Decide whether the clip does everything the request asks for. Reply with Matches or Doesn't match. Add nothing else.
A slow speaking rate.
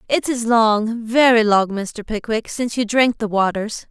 Doesn't match